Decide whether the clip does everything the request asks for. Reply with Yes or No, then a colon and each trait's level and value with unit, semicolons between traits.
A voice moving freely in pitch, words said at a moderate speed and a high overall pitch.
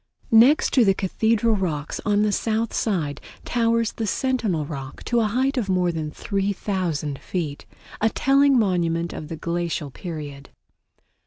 Yes: wide, 5.8 semitones; average, 150 wpm; high, 195 Hz